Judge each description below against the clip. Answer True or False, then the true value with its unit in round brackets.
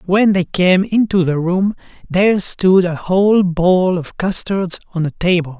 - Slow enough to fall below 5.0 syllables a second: True (4.4 syllables/s)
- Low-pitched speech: False (185 Hz)